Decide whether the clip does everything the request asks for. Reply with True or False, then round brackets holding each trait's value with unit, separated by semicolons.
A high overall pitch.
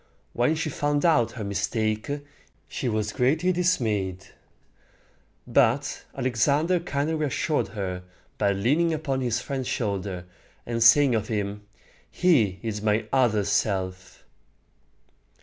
False (115 Hz)